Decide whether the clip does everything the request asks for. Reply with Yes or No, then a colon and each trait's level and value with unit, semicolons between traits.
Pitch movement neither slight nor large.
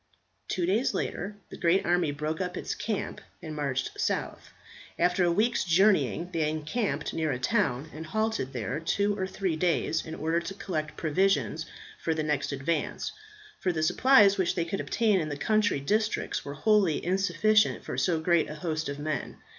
Yes: average, 4.2 semitones